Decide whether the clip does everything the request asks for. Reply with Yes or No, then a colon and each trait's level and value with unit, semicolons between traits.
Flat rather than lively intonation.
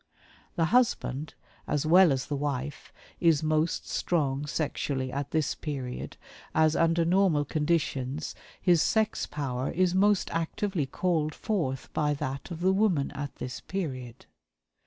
No: average, 3.9 semitones